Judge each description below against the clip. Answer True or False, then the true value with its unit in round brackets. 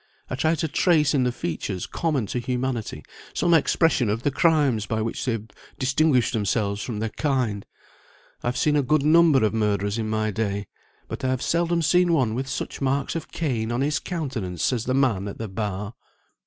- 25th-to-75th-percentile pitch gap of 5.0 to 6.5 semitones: True (5.5 semitones)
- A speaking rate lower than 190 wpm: False (200 wpm)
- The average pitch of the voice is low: True (125 Hz)